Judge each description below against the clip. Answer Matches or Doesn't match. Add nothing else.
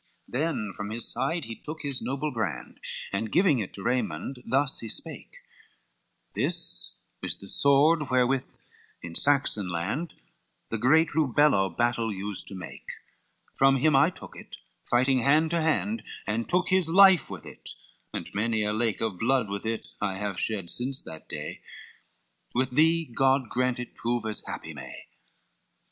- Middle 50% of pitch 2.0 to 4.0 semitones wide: Doesn't match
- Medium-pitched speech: Doesn't match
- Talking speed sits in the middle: Matches